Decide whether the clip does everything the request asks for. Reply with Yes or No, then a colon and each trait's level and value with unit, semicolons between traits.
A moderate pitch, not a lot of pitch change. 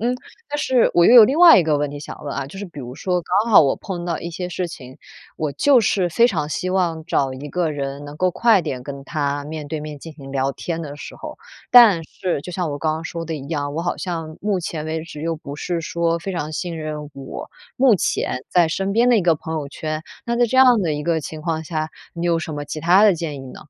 No: medium, 165 Hz; average, 3.6 semitones